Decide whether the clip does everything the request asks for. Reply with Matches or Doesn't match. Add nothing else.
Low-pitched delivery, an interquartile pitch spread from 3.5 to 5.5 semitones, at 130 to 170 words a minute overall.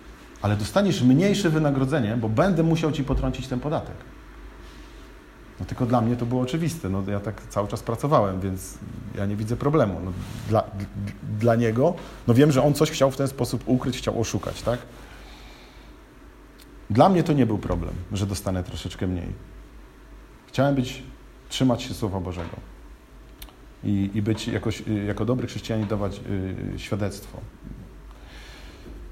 Matches